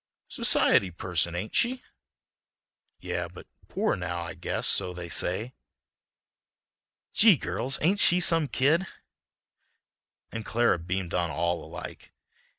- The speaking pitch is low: Yes, very low, 95 Hz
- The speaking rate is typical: No, slow, 120 wpm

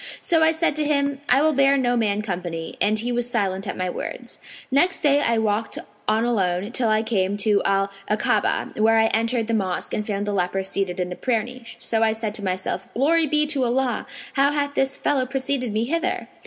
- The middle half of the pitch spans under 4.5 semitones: No, average, 5.2 semitones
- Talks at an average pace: No, fast, 220 wpm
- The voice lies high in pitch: Yes, high, 230 Hz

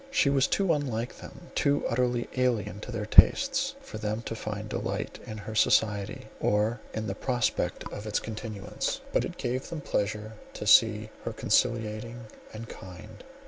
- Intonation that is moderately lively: Yes, average, 3.0 semitones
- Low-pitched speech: Yes, low, 110 Hz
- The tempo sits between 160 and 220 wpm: Yes, average, 165 wpm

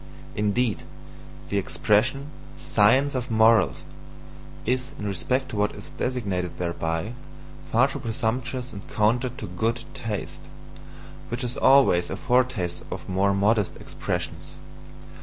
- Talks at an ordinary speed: No, slow, 120 wpm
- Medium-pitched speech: No, low, 110 Hz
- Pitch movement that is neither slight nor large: Yes, average, 4.3 semitones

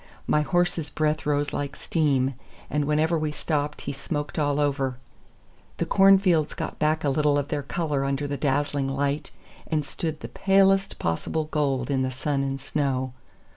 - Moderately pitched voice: Yes, medium, 145 Hz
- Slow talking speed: No, average, 170 wpm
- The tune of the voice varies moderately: No, narrow, 2.1 semitones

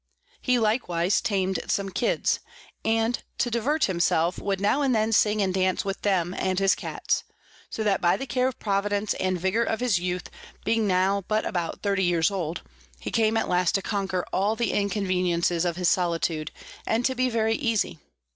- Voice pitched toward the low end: No, high, 195 Hz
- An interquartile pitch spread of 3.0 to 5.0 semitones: Yes, average, 3.5 semitones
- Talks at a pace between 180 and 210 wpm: Yes, average, 185 wpm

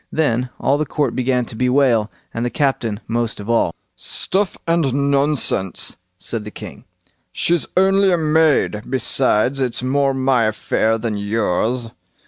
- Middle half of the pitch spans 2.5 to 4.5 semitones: Yes, average, 4.0 semitones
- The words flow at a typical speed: Yes, average, 145 wpm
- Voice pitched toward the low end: Yes, low, 125 Hz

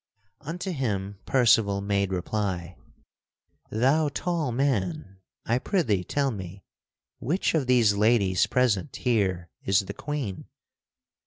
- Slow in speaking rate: Yes, slow, 110 wpm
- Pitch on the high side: No, low, 110 Hz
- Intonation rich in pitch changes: Yes, wide, 6.0 semitones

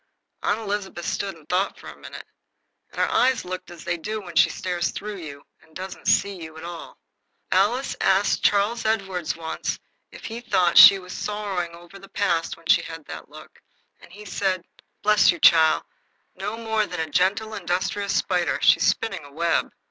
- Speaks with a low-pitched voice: No, medium, 185 Hz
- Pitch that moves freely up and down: No, average, 3.3 semitones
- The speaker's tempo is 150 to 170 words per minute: No, average, 185 wpm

